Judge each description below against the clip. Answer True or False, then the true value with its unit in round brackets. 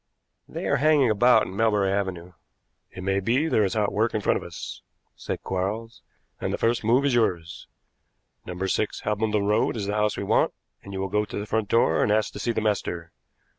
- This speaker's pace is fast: True (215 wpm)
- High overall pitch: False (105 Hz)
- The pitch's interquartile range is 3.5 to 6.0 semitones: False (2.6 semitones)